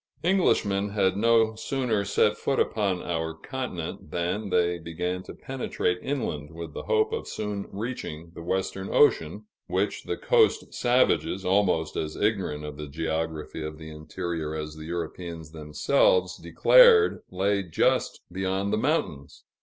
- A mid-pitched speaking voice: No, very low, 95 Hz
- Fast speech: No, average, 145 wpm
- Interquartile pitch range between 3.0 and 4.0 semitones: No, average, 5.0 semitones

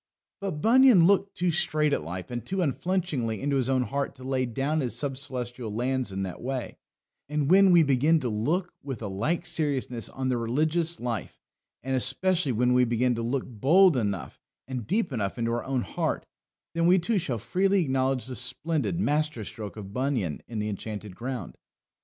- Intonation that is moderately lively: No, wide, 5.7 semitones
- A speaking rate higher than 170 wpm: Yes, average, 190 wpm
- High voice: No, low, 130 Hz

